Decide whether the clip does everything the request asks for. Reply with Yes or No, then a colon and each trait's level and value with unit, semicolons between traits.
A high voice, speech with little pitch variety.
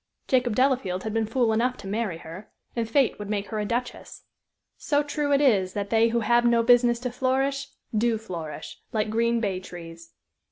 No: high, 230 Hz; average, 3.5 semitones